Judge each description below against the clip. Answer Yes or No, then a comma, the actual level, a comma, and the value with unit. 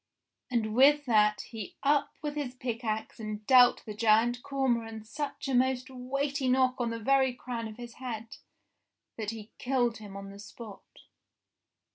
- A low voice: No, high, 240 Hz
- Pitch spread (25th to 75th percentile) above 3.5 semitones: No, average, 3.1 semitones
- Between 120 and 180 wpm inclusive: Yes, average, 165 wpm